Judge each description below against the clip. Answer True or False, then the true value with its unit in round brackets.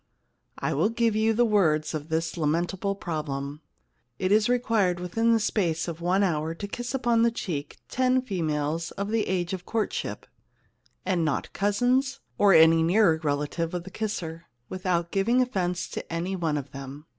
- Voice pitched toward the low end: False (180 Hz)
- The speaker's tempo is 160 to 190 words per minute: True (170 wpm)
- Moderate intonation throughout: True (4.9 semitones)